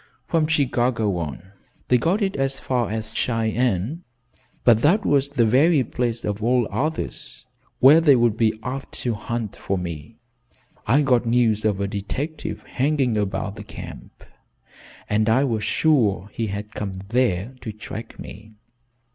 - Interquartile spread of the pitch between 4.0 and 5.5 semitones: Yes, average, 4.3 semitones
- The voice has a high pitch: No, low, 115 Hz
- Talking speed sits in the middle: Yes, average, 155 wpm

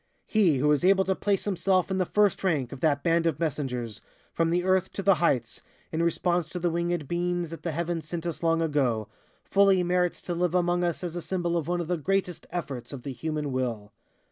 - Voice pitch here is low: No, medium, 170 Hz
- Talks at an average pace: No, fast, 225 wpm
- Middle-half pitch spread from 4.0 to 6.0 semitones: No, average, 3.1 semitones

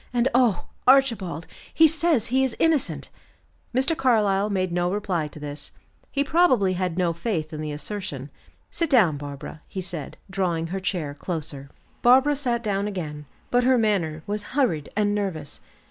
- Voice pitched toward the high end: Yes, high, 195 Hz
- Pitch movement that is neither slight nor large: No, wide, 7.4 semitones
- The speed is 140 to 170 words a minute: Yes, average, 160 wpm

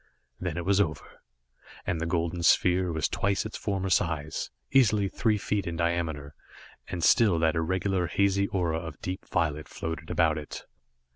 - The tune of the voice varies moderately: Yes, average, 3.1 semitones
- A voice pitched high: No, very low, 85 Hz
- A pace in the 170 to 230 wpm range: No, average, 160 wpm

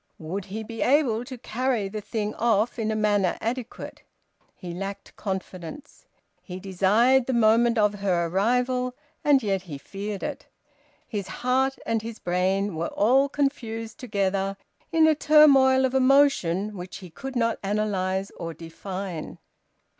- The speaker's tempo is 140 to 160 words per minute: Yes, average, 145 wpm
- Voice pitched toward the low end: No, high, 215 Hz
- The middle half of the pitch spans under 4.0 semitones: No, average, 4.7 semitones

